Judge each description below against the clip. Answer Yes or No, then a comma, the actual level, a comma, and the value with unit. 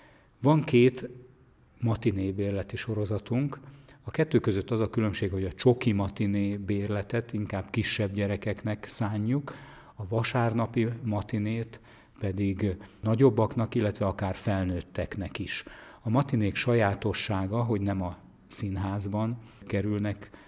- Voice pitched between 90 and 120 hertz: Yes, low, 110 Hz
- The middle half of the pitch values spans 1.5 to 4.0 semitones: Yes, average, 2.8 semitones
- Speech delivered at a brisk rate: No, average, 110 wpm